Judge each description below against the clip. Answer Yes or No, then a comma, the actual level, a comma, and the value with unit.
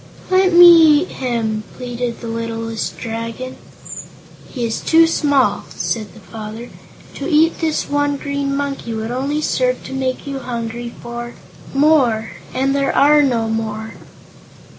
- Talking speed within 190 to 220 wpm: No, average, 140 wpm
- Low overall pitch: No, very high, 255 Hz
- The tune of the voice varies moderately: Yes, average, 4.0 semitones